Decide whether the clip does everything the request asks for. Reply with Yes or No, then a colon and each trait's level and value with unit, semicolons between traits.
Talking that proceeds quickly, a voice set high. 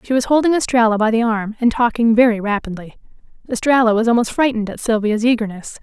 No: average, 185 wpm; high, 230 Hz